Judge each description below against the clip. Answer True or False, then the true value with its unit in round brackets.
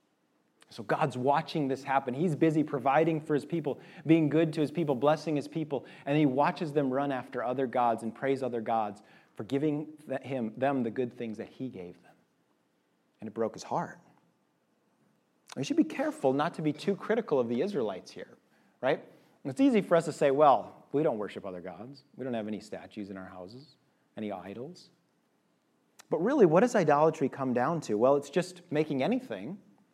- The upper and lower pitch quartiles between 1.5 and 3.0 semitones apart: False (4.4 semitones)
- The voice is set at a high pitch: False (140 Hz)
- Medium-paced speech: True (190 wpm)